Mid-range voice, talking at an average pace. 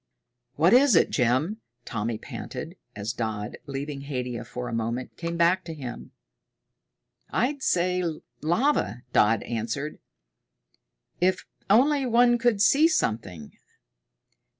No: medium, 150 Hz; slow, 115 wpm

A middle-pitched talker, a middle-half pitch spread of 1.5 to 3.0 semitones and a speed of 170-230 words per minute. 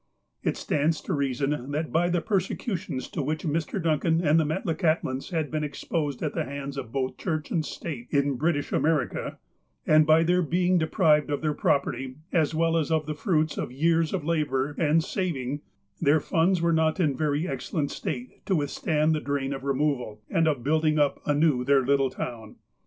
Yes: medium, 150 Hz; average, 2.7 semitones; average, 190 wpm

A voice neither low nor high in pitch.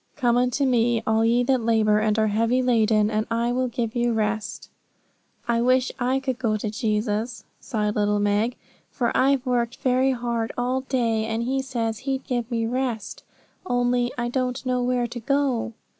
No: high, 240 Hz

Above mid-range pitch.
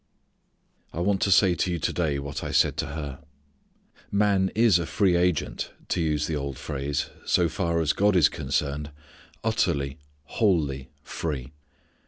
No: very low, 80 Hz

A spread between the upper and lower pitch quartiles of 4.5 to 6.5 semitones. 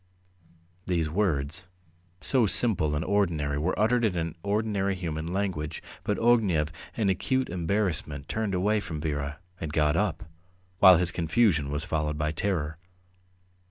Yes: average, 5.0 semitones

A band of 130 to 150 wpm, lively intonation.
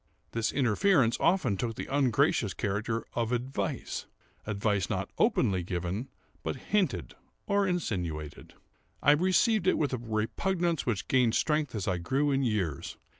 Yes: average, 140 wpm; wide, 6.9 semitones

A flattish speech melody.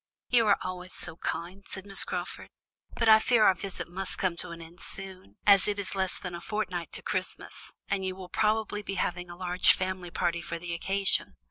Yes: narrow, 2.1 semitones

